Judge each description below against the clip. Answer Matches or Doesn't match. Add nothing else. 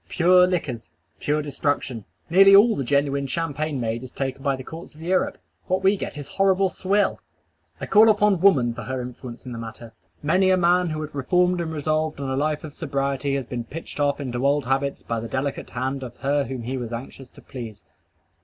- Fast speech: Matches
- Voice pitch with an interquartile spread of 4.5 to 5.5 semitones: Matches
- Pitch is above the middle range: Doesn't match